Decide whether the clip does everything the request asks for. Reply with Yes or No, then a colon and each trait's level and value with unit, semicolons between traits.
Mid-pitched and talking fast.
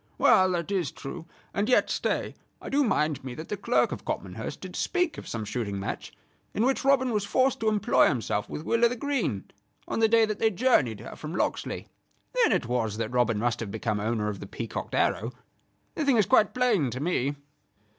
Yes: medium, 175 Hz; fast, 215 wpm